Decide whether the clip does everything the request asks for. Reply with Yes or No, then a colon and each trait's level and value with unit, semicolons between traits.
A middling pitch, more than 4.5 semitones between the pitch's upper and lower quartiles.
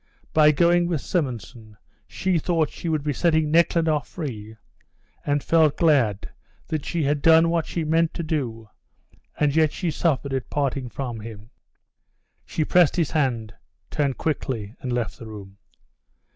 Yes: medium, 150 Hz; average, 5.1 semitones